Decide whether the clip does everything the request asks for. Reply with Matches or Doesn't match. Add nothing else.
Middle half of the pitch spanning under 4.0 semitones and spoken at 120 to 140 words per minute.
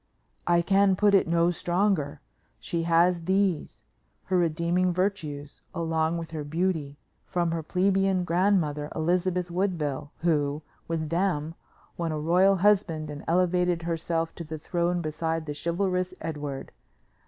Matches